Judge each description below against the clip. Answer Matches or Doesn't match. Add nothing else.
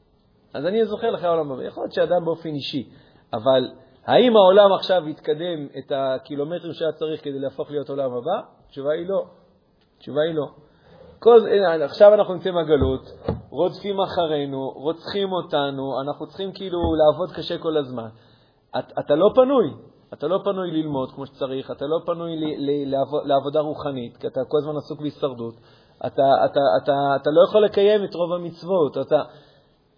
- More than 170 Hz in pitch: Doesn't match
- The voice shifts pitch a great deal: Doesn't match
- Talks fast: Matches